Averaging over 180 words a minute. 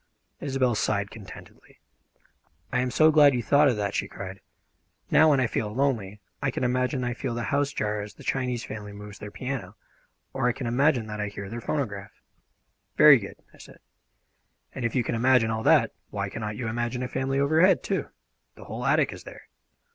Yes: average, 200 wpm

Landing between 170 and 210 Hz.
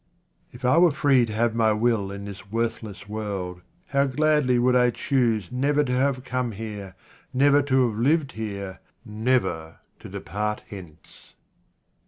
No: low, 115 Hz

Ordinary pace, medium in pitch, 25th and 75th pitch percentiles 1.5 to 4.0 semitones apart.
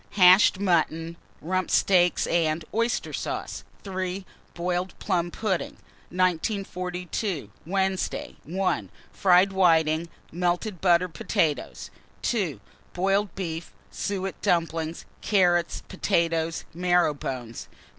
No: slow, 95 wpm; medium, 180 Hz; narrow, 2.5 semitones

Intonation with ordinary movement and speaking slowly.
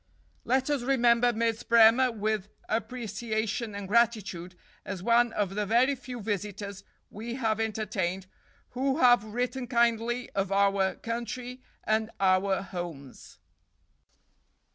Yes: average, 3.3 semitones; slow, 120 wpm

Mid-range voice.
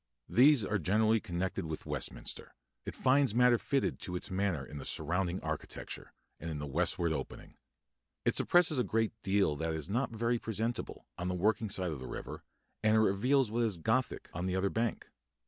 No: low, 100 Hz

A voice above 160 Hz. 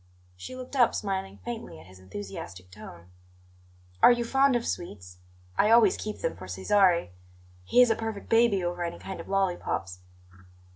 Yes: high, 190 Hz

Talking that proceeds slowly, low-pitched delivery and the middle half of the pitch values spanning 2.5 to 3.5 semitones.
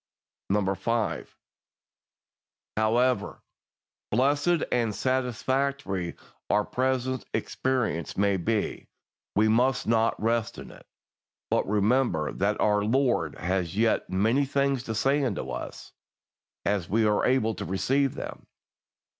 No: slow, 115 wpm; low, 115 Hz; average, 4.1 semitones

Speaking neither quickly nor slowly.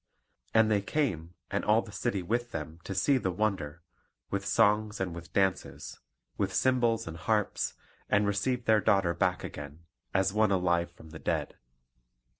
Yes: average, 165 wpm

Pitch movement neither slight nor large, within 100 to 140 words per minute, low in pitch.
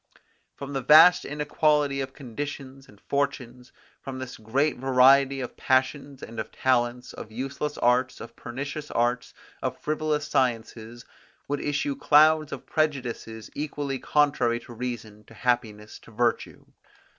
Yes: average, 3.2 semitones; slow, 135 wpm; low, 130 Hz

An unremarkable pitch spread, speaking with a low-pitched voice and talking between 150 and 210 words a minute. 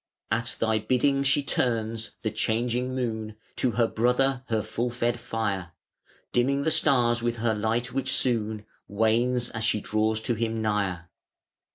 No: narrow, 2.1 semitones; low, 115 Hz; average, 155 wpm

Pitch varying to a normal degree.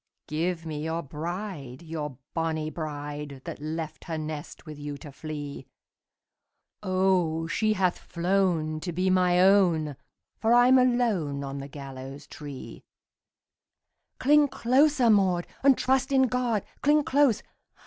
No: wide, 6.1 semitones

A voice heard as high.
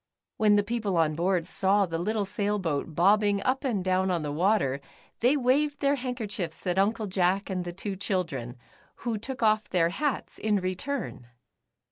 Yes: high, 200 Hz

